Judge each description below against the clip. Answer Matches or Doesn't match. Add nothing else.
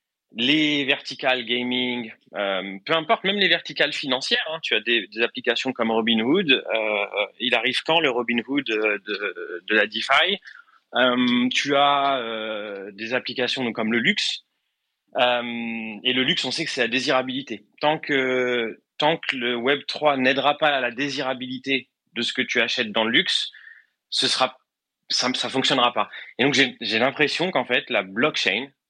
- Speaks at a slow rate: Doesn't match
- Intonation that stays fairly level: Doesn't match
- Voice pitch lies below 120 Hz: Doesn't match